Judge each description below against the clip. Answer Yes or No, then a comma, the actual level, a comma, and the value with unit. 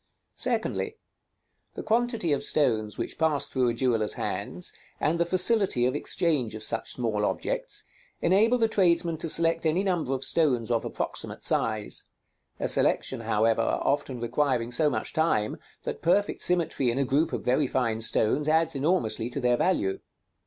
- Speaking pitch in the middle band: Yes, medium, 145 Hz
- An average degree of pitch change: No, wide, 6.1 semitones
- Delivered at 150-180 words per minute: Yes, average, 160 wpm